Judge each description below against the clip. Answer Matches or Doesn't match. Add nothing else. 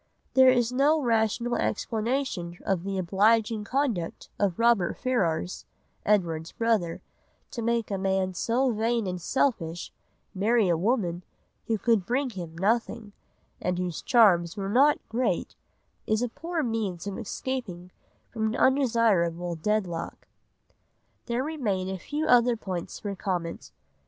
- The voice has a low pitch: Doesn't match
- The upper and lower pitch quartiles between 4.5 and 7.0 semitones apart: Matches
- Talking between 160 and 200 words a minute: Doesn't match